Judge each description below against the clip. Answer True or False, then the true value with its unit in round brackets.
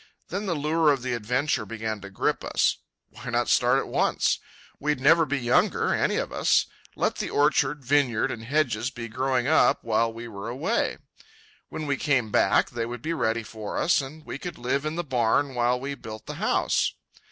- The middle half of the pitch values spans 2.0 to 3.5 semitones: False (3.9 semitones)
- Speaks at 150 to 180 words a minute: False (195 wpm)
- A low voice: True (125 Hz)